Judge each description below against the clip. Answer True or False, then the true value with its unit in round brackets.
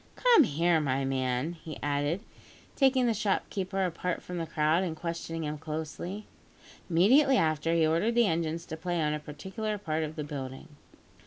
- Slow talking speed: False (170 wpm)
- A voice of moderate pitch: True (165 Hz)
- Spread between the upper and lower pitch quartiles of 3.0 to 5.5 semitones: True (3.9 semitones)